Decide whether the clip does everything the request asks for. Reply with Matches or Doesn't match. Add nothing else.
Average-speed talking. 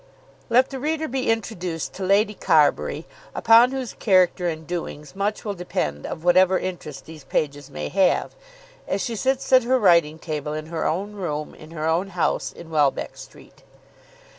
Matches